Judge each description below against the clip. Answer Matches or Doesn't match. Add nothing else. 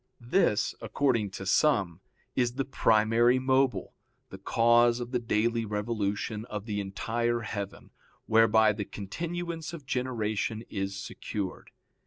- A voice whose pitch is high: Doesn't match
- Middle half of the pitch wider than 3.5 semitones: Doesn't match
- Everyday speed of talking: Doesn't match